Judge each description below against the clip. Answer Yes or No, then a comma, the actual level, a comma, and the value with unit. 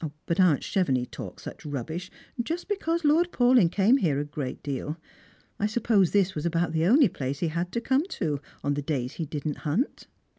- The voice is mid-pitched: Yes, medium, 170 Hz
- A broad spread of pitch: Yes, wide, 8.2 semitones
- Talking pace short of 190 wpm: No, average, 195 wpm